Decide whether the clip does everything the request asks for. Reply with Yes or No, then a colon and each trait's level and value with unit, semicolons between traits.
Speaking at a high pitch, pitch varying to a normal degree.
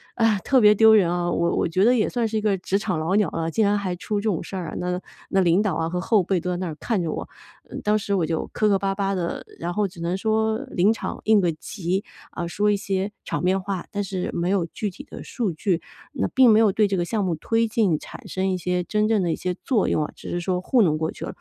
Yes: high, 195 Hz; average, 3.2 semitones